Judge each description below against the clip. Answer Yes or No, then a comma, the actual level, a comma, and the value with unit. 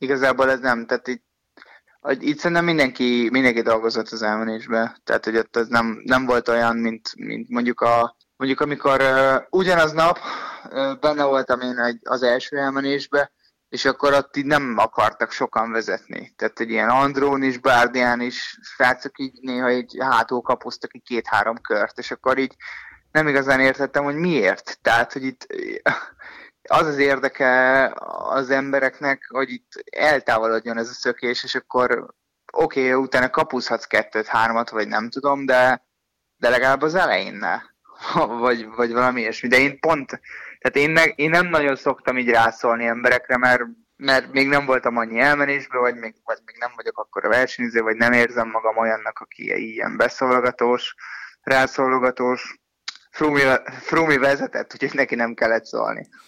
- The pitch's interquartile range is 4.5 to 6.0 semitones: No, average, 2.8 semitones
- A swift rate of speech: Yes, fast, 160 wpm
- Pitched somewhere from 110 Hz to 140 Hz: Yes, low, 130 Hz